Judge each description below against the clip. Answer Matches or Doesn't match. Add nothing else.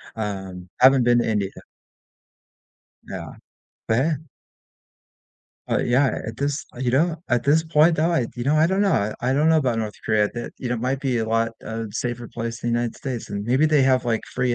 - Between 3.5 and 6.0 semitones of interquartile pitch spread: Matches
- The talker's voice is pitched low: Matches